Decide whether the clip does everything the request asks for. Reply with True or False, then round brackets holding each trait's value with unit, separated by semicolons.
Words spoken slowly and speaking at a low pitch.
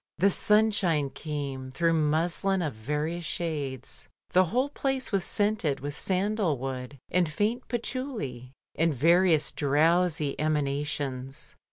False (120 wpm; 160 Hz)